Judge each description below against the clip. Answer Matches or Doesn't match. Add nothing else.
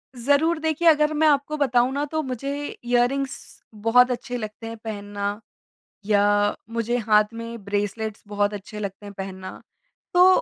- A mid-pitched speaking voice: Doesn't match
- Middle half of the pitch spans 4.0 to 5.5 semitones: Matches